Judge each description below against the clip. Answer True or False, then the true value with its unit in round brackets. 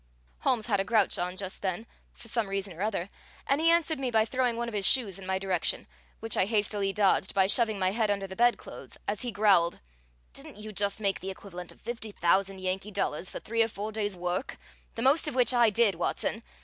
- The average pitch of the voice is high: True (205 Hz)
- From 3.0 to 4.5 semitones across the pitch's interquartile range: True (3.3 semitones)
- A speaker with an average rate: False (225 wpm)